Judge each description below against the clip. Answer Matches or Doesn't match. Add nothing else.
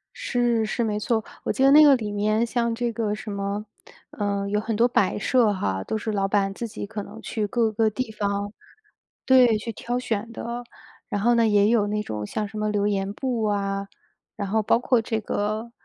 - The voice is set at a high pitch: Matches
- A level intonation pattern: Matches